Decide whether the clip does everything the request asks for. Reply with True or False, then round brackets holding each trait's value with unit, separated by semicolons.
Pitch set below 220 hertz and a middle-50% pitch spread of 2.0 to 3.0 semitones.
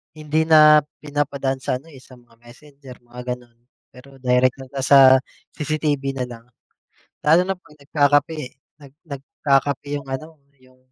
True (140 Hz; 2.7 semitones)